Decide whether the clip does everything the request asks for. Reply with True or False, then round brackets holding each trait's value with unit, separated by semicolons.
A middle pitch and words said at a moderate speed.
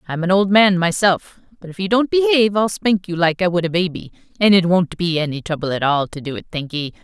False (180 Hz; 255 wpm)